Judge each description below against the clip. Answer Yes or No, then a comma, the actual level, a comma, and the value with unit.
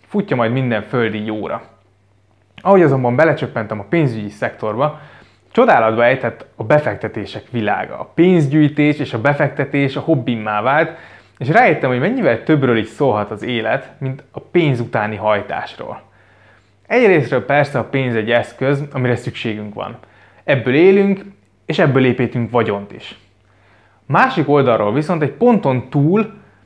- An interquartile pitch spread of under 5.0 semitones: No, wide, 5.4 semitones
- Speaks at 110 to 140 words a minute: Yes, average, 135 wpm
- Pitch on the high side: No, low, 125 Hz